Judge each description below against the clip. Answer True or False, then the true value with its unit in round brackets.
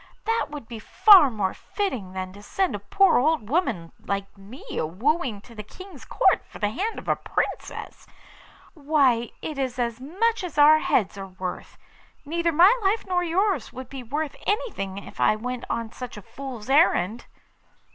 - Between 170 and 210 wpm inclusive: True (180 wpm)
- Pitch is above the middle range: True (260 Hz)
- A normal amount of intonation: False (8.3 semitones)